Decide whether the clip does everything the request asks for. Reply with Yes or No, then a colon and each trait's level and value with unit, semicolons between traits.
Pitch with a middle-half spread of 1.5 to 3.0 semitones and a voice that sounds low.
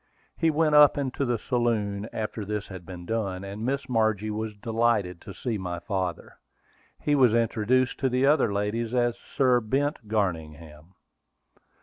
No: average, 4.0 semitones; low, 110 Hz